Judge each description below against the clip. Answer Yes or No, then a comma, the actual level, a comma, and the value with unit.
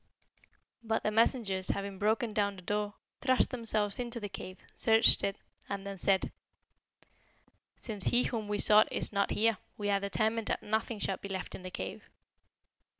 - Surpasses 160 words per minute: Yes, average, 170 wpm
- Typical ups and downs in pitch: No, narrow, 2.0 semitones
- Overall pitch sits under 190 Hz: No, high, 210 Hz